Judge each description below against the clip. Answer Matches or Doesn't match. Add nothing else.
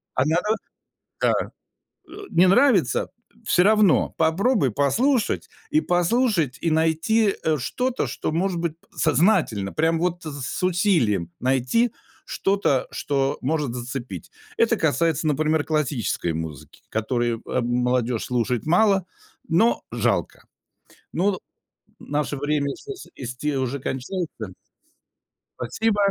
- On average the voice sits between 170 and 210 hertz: Doesn't match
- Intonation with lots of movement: Matches